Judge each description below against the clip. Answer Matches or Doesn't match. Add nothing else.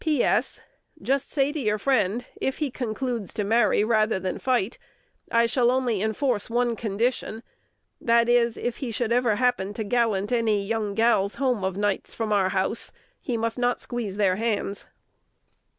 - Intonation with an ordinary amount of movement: Matches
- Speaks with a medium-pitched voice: Doesn't match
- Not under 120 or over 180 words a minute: Matches